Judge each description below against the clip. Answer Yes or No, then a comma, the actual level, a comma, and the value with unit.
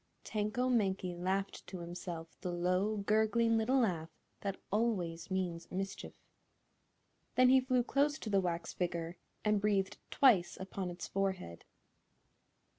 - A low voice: No, high, 195 Hz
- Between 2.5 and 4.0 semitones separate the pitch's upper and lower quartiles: Yes, average, 3.7 semitones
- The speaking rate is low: Yes, slow, 130 wpm